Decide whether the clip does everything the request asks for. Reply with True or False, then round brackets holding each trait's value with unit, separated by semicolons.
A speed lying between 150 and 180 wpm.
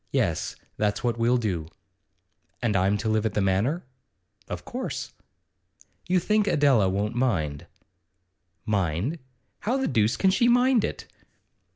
False (140 wpm)